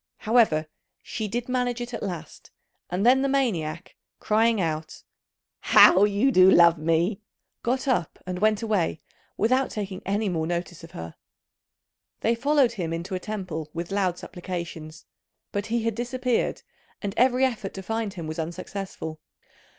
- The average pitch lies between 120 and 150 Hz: No, high, 200 Hz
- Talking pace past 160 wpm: No, average, 155 wpm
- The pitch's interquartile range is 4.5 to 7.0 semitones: Yes, wide, 5.4 semitones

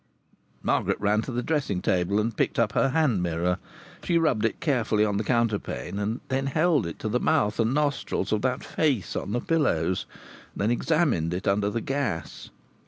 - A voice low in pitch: Yes, low, 115 Hz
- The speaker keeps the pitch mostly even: No, average, 5.2 semitones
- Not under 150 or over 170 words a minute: No, average, 190 wpm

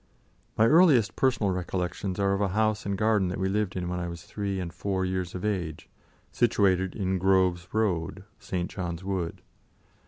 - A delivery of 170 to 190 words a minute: Yes, average, 180 wpm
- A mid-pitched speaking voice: No, very low, 95 Hz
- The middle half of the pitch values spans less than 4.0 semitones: Yes, narrow, 2.4 semitones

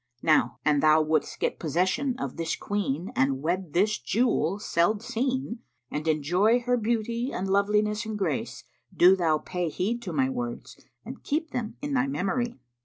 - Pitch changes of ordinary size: No, wide, 6.6 semitones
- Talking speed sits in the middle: Yes, average, 170 wpm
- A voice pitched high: Yes, high, 205 Hz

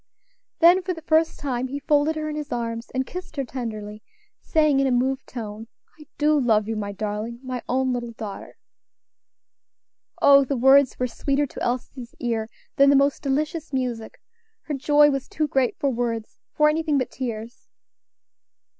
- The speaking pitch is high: Yes, very high, 265 Hz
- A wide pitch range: No, average, 3.9 semitones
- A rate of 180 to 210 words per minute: No, average, 170 wpm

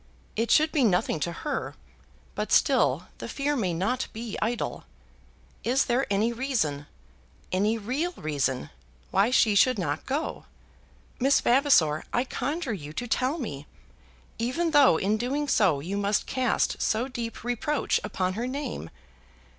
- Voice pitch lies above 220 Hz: Yes, high, 235 Hz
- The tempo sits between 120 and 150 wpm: Yes, average, 145 wpm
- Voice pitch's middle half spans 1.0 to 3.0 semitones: No, wide, 5.6 semitones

